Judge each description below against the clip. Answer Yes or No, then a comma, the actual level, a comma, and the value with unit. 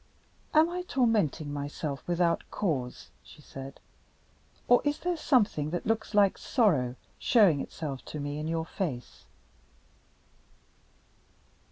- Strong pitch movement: Yes, wide, 7.7 semitones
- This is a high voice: No, medium, 165 Hz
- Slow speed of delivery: Yes, slow, 120 wpm